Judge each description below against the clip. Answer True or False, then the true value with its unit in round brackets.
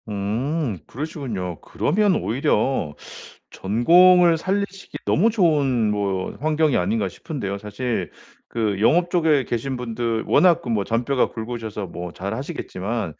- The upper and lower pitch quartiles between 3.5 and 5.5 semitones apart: False (7.3 semitones)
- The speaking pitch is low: True (120 Hz)